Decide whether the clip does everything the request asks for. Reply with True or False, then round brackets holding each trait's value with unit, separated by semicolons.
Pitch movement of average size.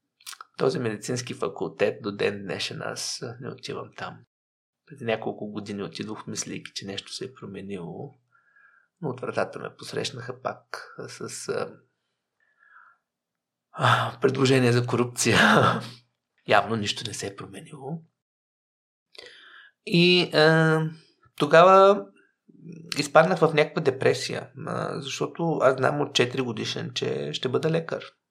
False (5.9 semitones)